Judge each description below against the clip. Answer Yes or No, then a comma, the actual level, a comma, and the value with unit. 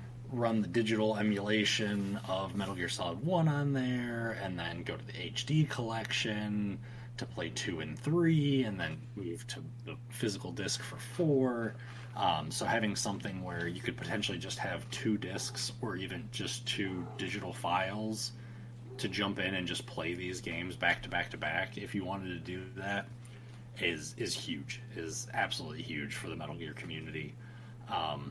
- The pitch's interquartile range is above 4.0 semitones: No, average, 3.3 semitones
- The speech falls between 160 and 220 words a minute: Yes, average, 170 wpm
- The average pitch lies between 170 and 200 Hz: No, low, 120 Hz